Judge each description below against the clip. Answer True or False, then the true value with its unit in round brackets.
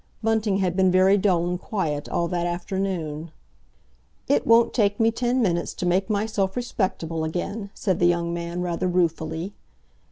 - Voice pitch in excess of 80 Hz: True (185 Hz)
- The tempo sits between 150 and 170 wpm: True (160 wpm)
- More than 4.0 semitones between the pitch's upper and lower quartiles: False (3.1 semitones)